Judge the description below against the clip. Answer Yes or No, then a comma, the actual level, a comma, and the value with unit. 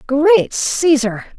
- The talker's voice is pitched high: Yes, very high, 295 Hz